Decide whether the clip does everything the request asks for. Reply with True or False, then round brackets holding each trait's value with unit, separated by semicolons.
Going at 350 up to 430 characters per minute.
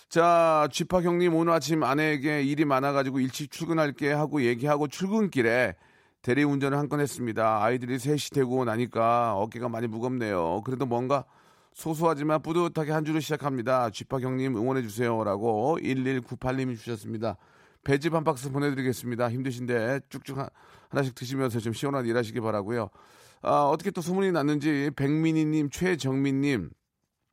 True (360 characters per minute)